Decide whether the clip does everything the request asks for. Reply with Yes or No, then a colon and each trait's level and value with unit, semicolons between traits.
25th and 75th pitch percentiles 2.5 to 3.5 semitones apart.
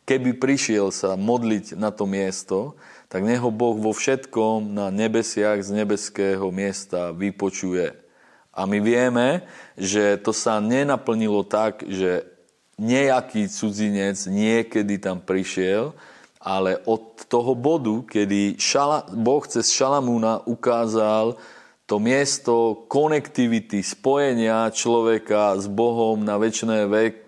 Yes: average, 2.8 semitones